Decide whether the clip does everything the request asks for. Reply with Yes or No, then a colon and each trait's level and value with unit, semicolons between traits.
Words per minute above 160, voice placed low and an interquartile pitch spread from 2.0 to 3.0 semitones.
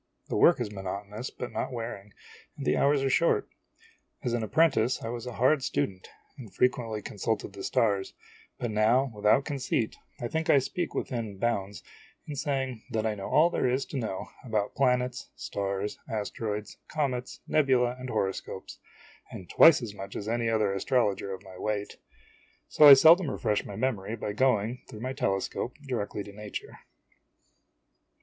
No: average, 170 wpm; low, 115 Hz; average, 4.1 semitones